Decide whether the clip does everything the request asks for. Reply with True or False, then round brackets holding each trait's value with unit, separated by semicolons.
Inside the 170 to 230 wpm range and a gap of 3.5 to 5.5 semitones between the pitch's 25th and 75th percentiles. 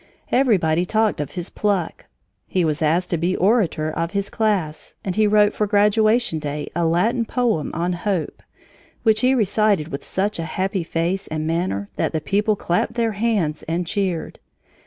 True (175 wpm; 4.6 semitones)